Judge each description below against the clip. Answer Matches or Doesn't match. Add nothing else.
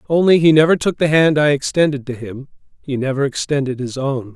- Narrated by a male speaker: Matches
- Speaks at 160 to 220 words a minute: Matches